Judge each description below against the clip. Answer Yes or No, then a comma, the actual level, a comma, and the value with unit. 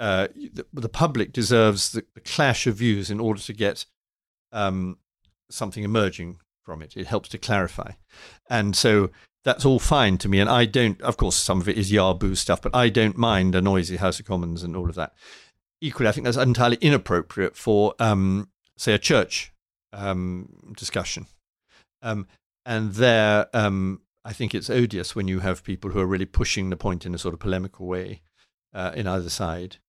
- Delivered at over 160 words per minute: Yes, average, 190 wpm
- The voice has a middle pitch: No, low, 100 Hz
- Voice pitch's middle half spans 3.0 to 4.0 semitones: Yes, average, 3.7 semitones